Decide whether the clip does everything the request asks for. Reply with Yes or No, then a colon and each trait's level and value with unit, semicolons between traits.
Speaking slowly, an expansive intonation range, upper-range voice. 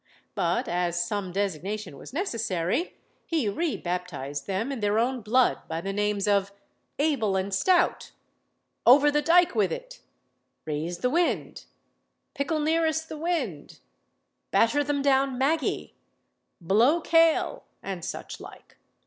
Yes: slow, 130 wpm; wide, 8.2 semitones; high, 230 Hz